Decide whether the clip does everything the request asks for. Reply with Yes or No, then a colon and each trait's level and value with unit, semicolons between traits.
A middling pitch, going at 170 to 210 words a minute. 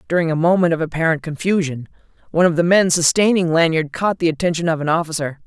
Yes: medium, 165 Hz; average, 200 wpm